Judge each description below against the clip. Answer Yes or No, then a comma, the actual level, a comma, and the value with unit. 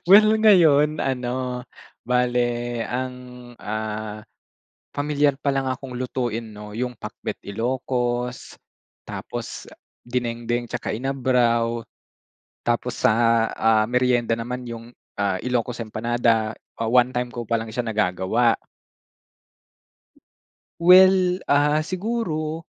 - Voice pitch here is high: No, low, 125 Hz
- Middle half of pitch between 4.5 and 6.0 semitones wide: No, average, 2.8 semitones